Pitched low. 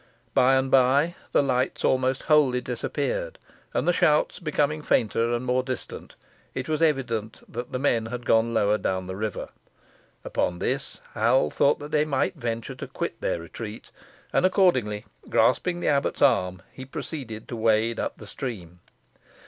Yes: low, 125 Hz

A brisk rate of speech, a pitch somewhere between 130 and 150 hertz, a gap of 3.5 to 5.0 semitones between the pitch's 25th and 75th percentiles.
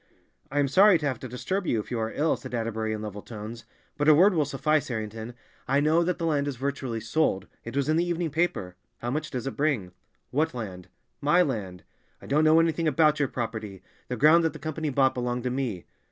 No: fast, 225 wpm; low, 135 Hz; wide, 5.4 semitones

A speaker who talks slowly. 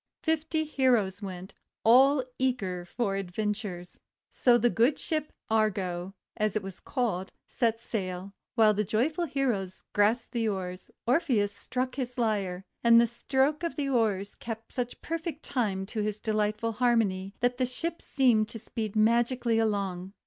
No: average, 150 wpm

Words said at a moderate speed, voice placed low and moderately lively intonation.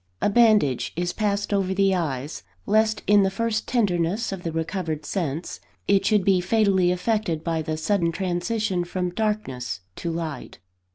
No: average, 160 wpm; medium, 185 Hz; average, 3.9 semitones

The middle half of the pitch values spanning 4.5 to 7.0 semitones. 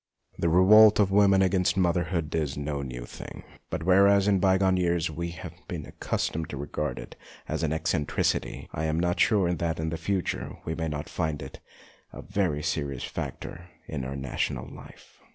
No: average, 3.7 semitones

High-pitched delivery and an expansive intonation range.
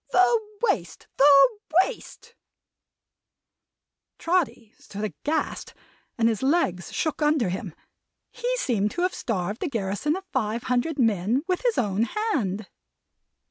Yes: very high, 250 Hz; wide, 7.8 semitones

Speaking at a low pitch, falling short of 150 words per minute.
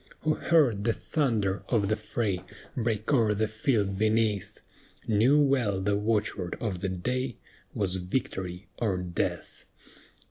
Yes: low, 105 Hz; slow, 135 wpm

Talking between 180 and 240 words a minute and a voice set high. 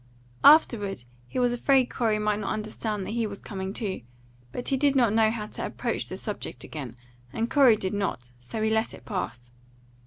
Yes: average, 195 wpm; high, 215 Hz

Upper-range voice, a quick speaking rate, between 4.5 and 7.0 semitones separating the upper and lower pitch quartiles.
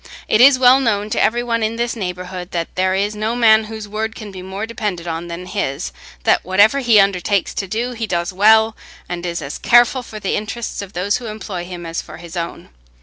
No: high, 205 Hz; fast, 225 wpm; average, 3.7 semitones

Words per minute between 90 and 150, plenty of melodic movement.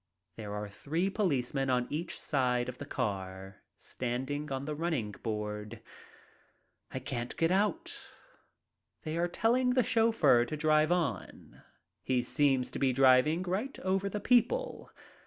Yes: average, 140 wpm; wide, 6.8 semitones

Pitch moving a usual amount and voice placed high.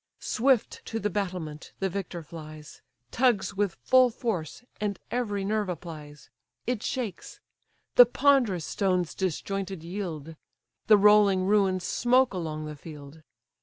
Yes: average, 4.4 semitones; high, 195 Hz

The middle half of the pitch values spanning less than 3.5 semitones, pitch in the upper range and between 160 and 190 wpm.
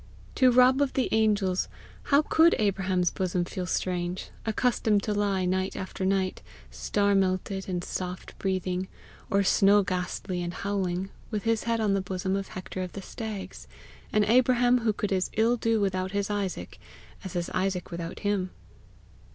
Yes: narrow, 2.6 semitones; high, 195 Hz; average, 165 wpm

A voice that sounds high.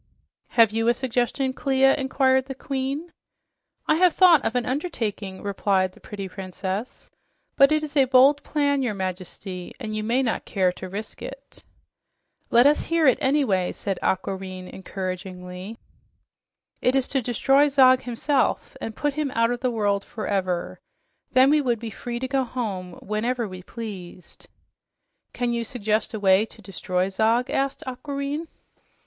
Yes: high, 235 Hz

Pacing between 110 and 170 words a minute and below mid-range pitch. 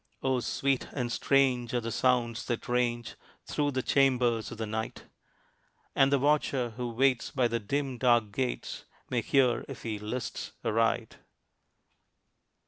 Yes: average, 145 wpm; low, 125 Hz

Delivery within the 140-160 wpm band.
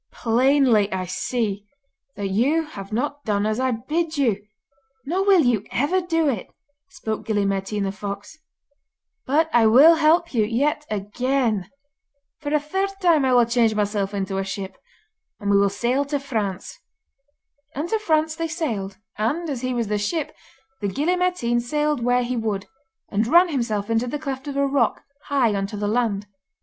No: average, 180 wpm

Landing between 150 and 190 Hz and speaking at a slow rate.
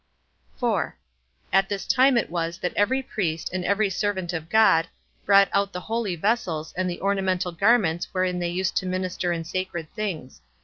No: medium, 185 Hz; average, 175 wpm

